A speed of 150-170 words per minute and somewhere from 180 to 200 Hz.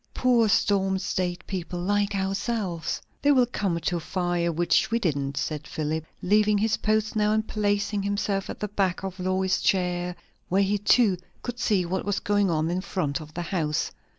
No: average, 185 wpm; high, 190 Hz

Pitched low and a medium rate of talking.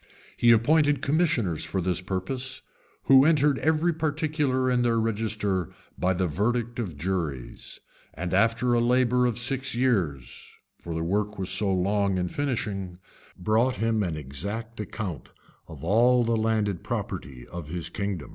Yes: low, 110 Hz; average, 150 wpm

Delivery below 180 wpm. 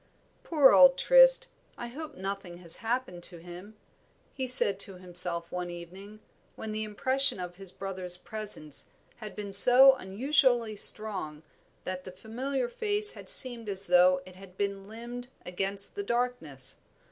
Yes: average, 150 wpm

